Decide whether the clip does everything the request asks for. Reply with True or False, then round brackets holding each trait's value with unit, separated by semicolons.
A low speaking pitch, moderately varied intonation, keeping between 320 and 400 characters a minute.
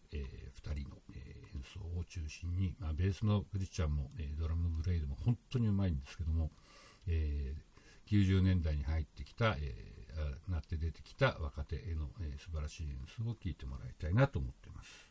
True (80 Hz; 4.2 semitones; 385 characters per minute)